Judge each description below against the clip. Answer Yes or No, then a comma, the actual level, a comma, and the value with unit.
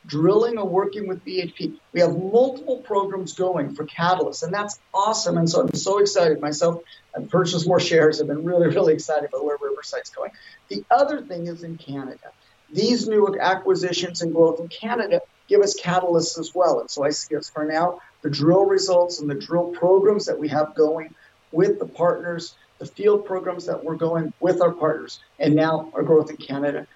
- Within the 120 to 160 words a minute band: No, average, 195 wpm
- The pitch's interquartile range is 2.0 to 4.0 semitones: Yes, average, 3.7 semitones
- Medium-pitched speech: Yes, medium, 175 Hz